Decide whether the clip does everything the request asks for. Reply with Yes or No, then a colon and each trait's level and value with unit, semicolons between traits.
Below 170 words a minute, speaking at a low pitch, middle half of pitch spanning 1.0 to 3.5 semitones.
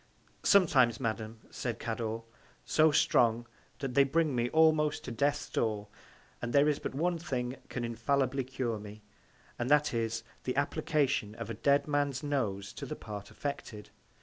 No: average, 160 wpm; low, 125 Hz; average, 4.1 semitones